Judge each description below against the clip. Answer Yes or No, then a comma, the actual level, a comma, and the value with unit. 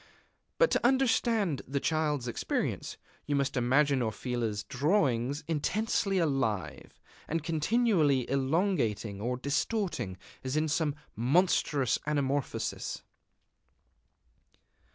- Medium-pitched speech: Yes, medium, 145 Hz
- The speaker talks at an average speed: No, slow, 90 wpm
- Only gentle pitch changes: No, average, 5.2 semitones